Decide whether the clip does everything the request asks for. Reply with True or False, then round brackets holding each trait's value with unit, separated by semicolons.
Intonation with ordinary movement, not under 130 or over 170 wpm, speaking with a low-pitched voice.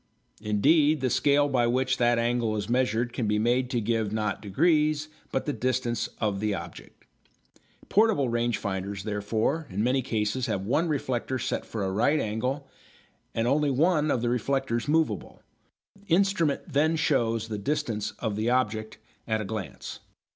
True (4.7 semitones; 165 wpm; 120 Hz)